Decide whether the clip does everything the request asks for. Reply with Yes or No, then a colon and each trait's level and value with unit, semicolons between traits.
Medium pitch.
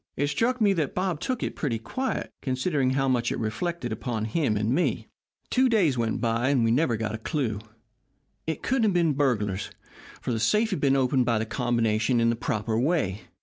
No: low, 130 Hz